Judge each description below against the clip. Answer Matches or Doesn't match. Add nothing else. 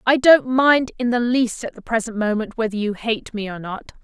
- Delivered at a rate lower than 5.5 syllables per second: Matches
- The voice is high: Matches